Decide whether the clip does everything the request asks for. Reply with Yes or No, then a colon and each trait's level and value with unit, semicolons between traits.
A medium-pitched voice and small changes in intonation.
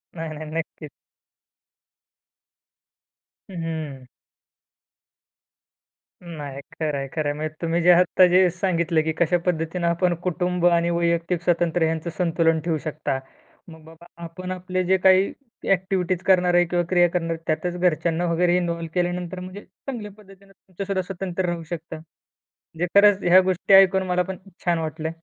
Yes: medium, 175 Hz; narrow, 2.0 semitones